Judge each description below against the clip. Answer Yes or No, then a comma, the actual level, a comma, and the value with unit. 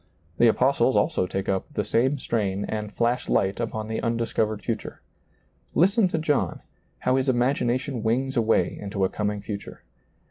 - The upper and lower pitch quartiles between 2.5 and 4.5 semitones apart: Yes, average, 3.9 semitones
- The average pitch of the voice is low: Yes, low, 115 Hz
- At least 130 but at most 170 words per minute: Yes, average, 155 wpm